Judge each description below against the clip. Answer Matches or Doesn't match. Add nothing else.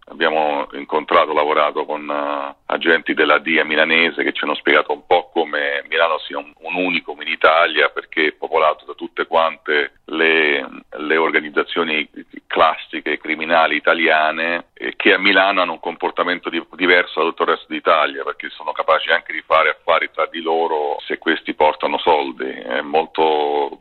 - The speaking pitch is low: Matches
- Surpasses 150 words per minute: Matches